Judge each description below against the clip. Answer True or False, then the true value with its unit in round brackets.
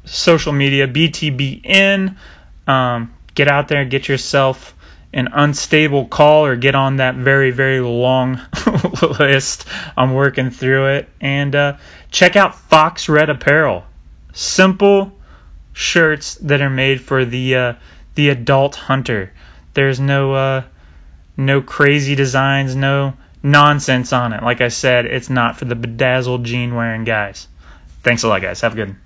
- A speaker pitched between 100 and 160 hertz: True (135 Hz)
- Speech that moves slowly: False (150 wpm)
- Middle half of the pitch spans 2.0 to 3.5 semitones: True (2.9 semitones)